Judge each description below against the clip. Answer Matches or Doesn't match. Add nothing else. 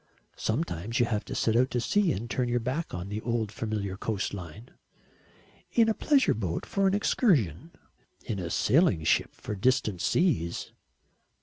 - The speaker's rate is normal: Matches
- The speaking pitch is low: Matches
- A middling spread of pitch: Doesn't match